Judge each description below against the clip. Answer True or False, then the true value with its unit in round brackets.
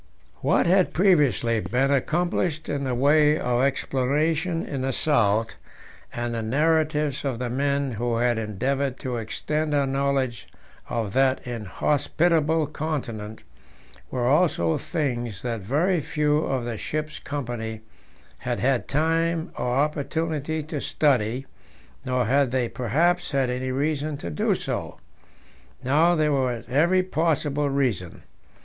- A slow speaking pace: True (130 wpm)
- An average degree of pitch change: True (4.0 semitones)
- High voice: False (140 Hz)